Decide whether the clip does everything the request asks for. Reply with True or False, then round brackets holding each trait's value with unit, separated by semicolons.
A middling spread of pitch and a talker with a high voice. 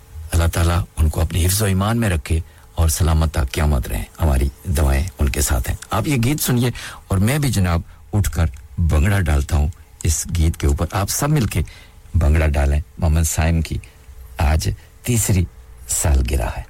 False (3.7 semitones; 85 Hz)